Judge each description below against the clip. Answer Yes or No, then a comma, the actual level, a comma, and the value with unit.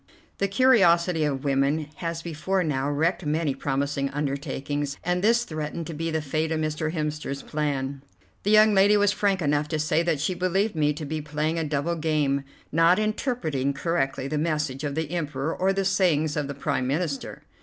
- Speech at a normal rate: Yes, average, 185 wpm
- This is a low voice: No, medium, 155 Hz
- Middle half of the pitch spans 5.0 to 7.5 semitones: No, average, 3.3 semitones